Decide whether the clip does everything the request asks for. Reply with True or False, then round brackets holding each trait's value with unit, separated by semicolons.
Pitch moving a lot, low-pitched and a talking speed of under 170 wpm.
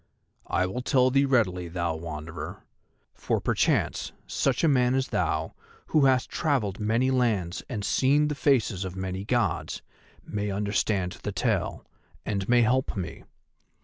True (5.8 semitones; 105 Hz; 150 wpm)